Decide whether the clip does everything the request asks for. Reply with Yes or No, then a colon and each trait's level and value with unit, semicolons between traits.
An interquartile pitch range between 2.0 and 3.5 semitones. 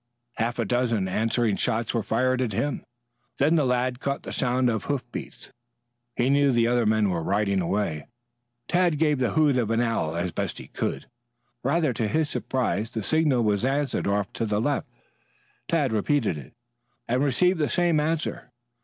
No: average, 4.8 semitones